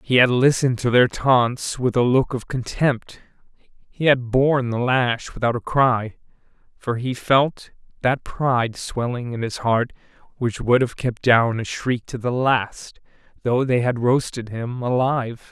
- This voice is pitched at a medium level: No, low, 125 Hz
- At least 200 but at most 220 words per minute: No, average, 170 wpm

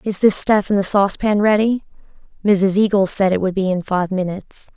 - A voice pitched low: No, high, 195 Hz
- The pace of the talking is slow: No, average, 200 wpm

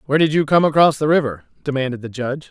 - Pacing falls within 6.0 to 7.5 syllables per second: Yes, 7.3 syllables/s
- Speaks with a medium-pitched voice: Yes, medium, 145 Hz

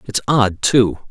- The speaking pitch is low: Yes, low, 110 Hz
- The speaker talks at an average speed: Yes, average, 165 wpm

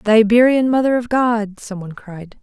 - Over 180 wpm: No, average, 175 wpm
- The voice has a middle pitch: No, high, 225 Hz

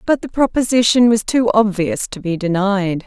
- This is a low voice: No, high, 215 Hz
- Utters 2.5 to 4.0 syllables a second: No, 4.9 syllables/s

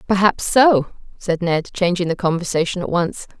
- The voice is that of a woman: Yes, female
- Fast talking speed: No, average, 160 wpm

